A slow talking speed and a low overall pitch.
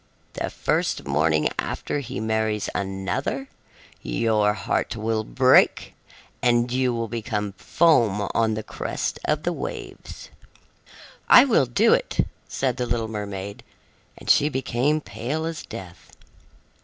Yes: slow, 130 wpm; low, 115 Hz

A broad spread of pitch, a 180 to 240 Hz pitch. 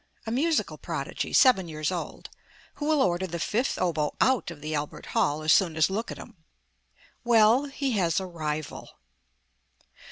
Yes: wide, 7.4 semitones; medium, 185 Hz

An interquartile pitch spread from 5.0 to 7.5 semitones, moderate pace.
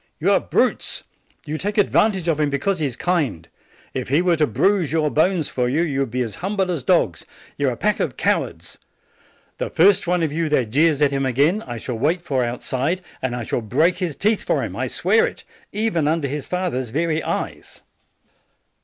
No: average, 5.3 semitones; fast, 215 wpm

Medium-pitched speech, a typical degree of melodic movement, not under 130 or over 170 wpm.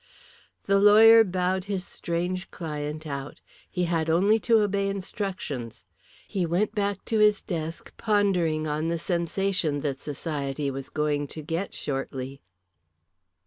Yes: medium, 170 Hz; average, 4.7 semitones; slow, 135 wpm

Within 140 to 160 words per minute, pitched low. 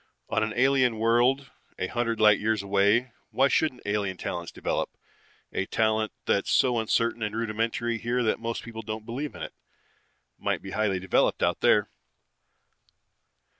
Yes: average, 150 wpm; low, 115 Hz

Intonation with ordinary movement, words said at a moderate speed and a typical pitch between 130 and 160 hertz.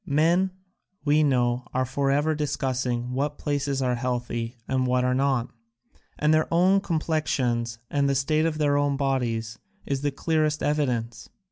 Yes: average, 3.2 semitones; average, 150 wpm; low, 135 Hz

